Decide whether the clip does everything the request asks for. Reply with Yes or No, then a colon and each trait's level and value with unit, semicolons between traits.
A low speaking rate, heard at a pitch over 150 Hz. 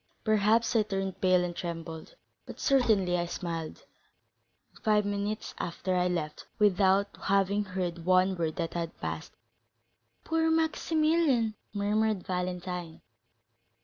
Yes: slow, 120 wpm; high, 190 Hz